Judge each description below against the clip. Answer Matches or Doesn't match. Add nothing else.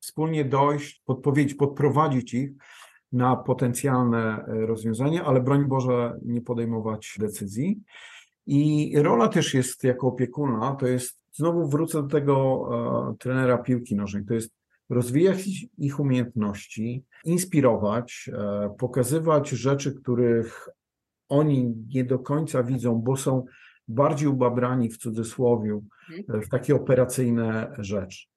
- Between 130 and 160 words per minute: Doesn't match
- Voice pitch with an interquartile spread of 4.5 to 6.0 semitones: Doesn't match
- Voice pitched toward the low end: Matches